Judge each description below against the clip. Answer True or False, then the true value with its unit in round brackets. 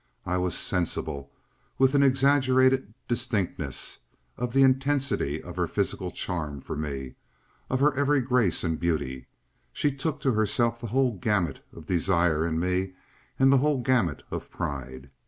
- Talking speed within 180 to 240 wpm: False (155 wpm)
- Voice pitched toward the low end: True (105 Hz)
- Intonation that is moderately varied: False (8.4 semitones)